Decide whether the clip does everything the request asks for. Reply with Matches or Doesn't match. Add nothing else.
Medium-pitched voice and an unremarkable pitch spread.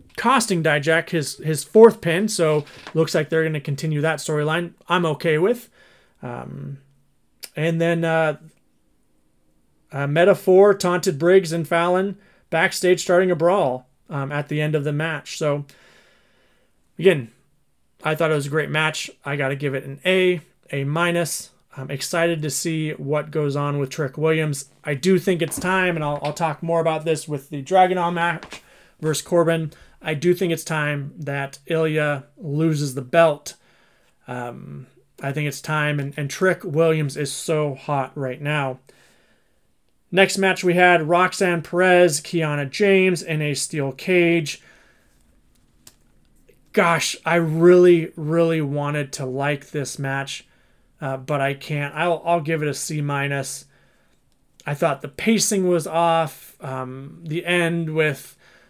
Matches